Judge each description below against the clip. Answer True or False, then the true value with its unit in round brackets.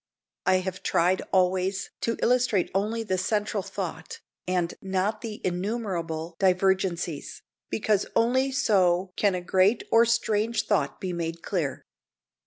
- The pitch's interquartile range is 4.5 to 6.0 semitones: False (3.1 semitones)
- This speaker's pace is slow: True (130 wpm)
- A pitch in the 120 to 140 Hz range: False (190 Hz)